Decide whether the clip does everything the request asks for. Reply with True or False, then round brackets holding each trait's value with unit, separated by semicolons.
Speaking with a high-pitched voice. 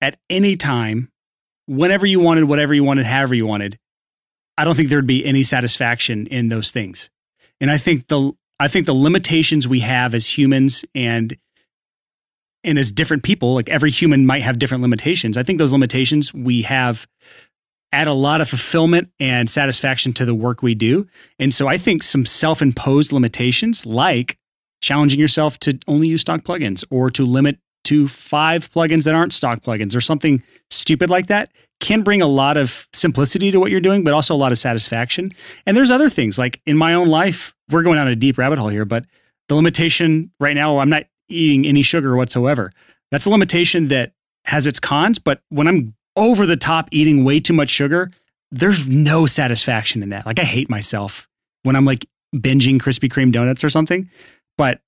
False (140 Hz)